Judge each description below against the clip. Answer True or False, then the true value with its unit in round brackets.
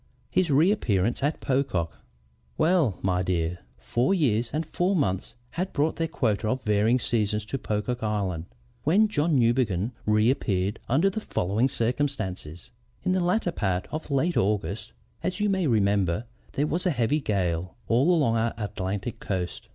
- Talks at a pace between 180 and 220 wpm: False (155 wpm)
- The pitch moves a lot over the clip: True (7.3 semitones)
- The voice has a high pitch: False (115 Hz)